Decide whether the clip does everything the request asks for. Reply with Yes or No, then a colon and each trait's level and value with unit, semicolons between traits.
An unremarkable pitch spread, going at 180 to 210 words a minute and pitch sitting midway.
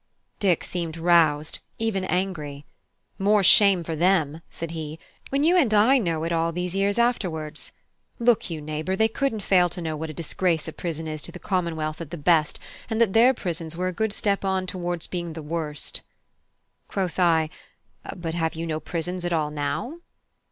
Yes: average, 3.4 semitones; average, 195 wpm; medium, 175 Hz